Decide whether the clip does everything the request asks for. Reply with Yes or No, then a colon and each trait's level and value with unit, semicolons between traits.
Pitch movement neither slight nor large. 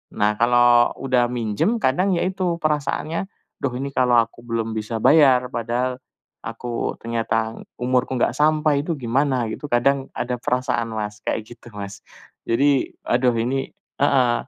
Yes: average, 3.0 semitones